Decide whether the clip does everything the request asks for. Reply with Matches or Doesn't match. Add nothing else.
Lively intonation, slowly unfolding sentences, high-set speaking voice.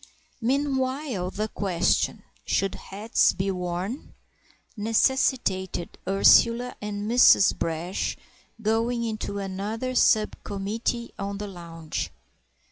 Doesn't match